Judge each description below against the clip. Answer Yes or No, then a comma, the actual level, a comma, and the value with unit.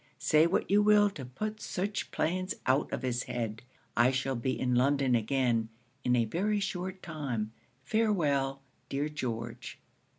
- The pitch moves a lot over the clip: Yes, wide, 7.0 semitones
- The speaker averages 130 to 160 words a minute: Yes, average, 155 wpm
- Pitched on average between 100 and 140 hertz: Yes, low, 135 Hz